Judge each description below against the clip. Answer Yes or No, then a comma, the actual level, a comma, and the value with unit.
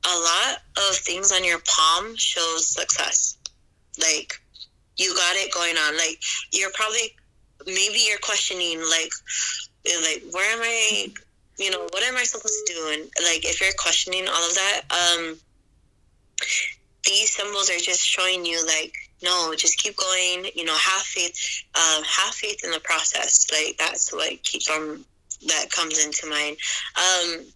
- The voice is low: No, medium, 180 Hz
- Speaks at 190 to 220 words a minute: No, average, 160 wpm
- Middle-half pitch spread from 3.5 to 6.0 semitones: No, average, 3.1 semitones